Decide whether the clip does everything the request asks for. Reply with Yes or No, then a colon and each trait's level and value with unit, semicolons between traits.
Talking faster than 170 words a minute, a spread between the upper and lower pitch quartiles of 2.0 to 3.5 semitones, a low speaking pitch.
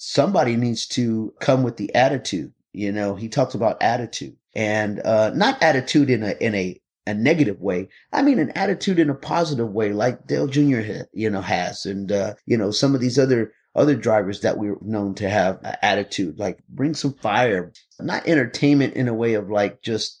No: average, 200 wpm; average, 4.9 semitones; low, 115 Hz